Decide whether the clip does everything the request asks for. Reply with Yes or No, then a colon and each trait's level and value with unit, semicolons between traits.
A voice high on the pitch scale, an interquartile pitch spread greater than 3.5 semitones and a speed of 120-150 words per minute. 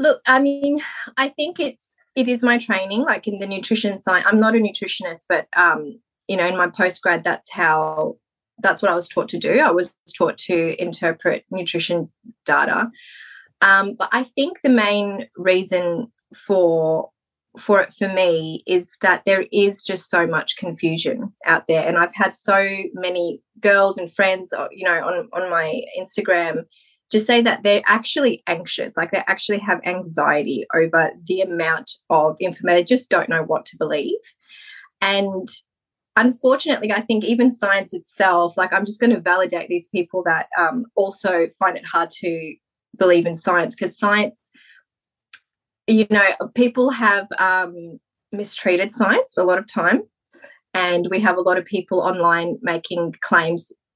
No: high, 195 Hz; average, 4.2 semitones; average, 165 wpm